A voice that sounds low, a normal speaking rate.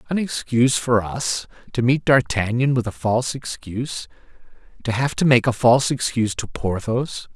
Yes: low, 120 Hz; average, 165 wpm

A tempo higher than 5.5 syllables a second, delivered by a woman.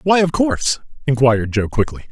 No: 5.8 syllables/s; male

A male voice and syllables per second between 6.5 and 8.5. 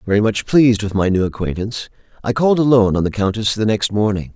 Yes: male; 6.7 syllables/s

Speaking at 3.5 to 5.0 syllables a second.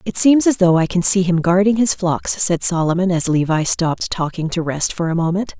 No: 5.3 syllables/s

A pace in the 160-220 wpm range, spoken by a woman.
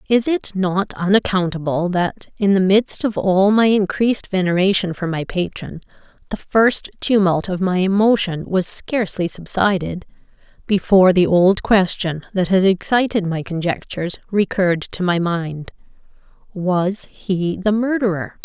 No: slow, 135 wpm; female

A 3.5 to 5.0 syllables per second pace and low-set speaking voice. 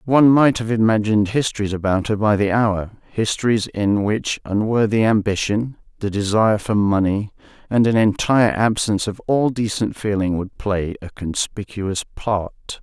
Yes: 4.8 syllables/s; low, 105 Hz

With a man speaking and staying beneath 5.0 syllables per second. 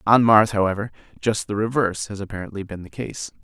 No: male; 6.1 syllables/s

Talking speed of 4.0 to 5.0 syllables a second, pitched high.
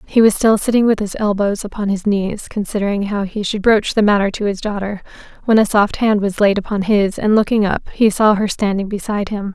No: 5.6 syllables/s; high, 205 Hz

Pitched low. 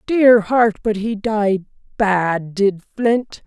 No: high, 210 Hz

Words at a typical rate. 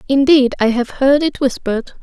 Yes: average, 180 wpm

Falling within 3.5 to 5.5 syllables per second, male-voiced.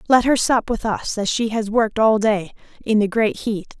No: 4.9 syllables/s; female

